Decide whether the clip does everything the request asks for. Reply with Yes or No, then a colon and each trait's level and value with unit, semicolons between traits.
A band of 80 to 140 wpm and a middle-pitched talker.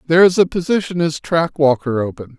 No: average, 200 wpm; medium, 155 Hz